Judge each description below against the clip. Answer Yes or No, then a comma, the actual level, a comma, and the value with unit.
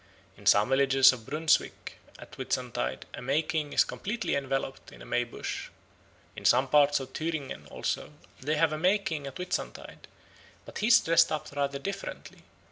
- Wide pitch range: No, average, 3.4 semitones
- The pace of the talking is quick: No, average, 175 wpm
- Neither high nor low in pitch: Yes, medium, 145 Hz